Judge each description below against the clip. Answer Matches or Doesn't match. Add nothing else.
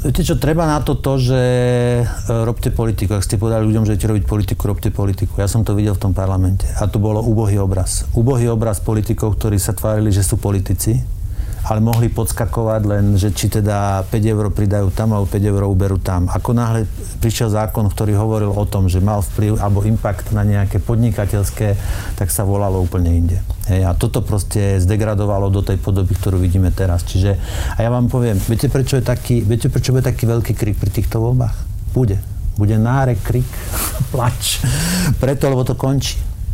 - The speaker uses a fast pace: Matches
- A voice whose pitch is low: Matches